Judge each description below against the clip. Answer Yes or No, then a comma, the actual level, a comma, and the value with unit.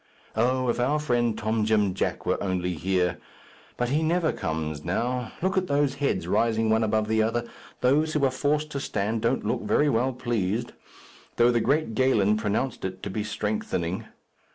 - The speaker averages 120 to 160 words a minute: No, average, 180 wpm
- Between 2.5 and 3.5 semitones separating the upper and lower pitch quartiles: No, average, 4.1 semitones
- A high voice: No, low, 115 Hz